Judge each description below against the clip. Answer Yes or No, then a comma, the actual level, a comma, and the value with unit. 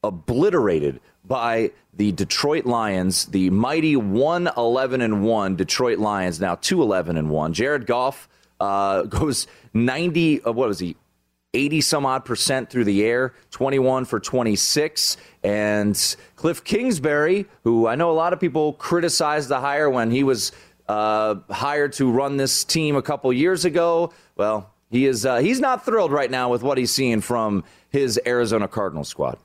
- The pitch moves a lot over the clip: Yes, wide, 6.1 semitones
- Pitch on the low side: Yes, low, 125 Hz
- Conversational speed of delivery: Yes, average, 165 wpm